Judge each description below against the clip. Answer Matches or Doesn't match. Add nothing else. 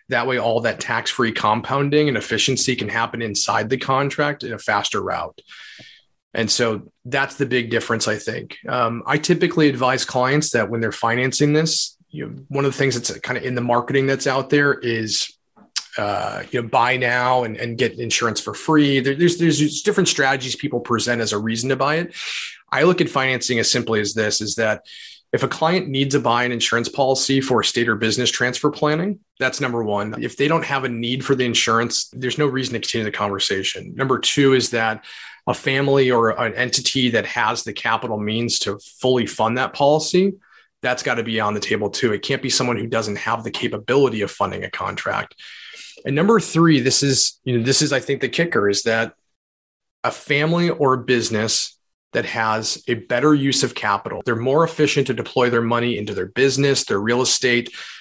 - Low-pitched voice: Matches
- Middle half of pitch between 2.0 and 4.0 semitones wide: Matches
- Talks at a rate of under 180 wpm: Doesn't match